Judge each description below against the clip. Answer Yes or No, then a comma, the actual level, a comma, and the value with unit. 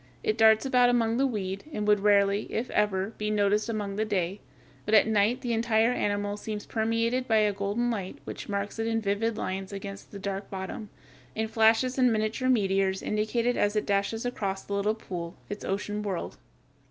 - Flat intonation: Yes, narrow, 2.2 semitones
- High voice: Yes, high, 210 Hz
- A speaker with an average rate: Yes, average, 195 wpm